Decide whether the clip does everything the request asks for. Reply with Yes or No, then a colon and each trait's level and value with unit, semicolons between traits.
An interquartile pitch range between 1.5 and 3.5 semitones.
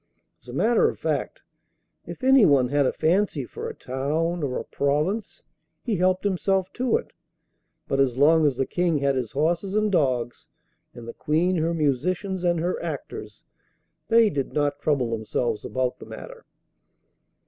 No: wide, 5.6 semitones